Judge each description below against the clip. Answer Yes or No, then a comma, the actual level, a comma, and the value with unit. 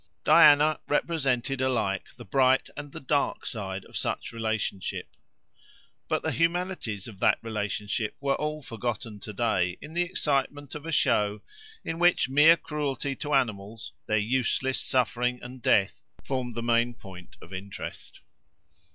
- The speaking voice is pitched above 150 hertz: No, low, 125 Hz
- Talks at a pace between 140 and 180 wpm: Yes, average, 145 wpm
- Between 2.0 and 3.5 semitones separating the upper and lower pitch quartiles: No, average, 5.3 semitones